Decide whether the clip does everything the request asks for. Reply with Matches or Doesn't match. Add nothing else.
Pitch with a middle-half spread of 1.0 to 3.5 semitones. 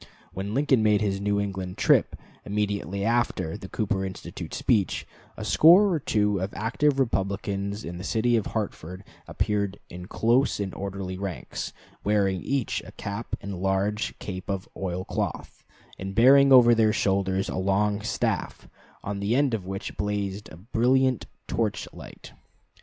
Matches